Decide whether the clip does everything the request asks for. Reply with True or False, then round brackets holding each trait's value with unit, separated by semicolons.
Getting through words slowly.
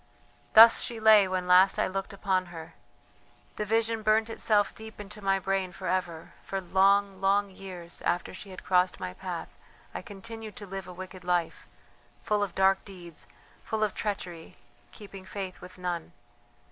False (170 wpm)